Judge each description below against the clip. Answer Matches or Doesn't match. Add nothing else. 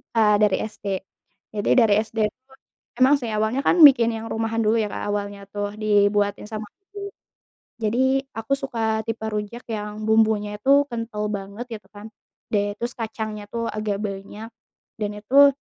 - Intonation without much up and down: Matches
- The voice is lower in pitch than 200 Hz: Doesn't match